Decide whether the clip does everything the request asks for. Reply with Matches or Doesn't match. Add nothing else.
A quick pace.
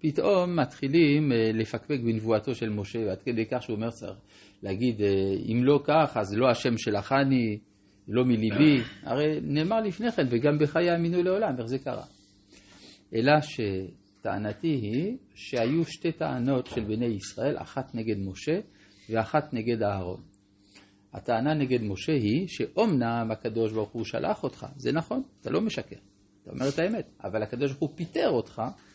Matches